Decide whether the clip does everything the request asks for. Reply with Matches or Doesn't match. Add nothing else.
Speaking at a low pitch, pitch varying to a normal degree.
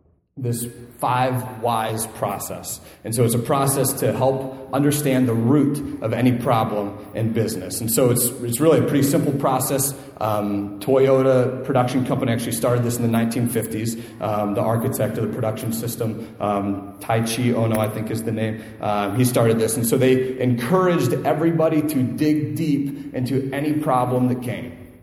Matches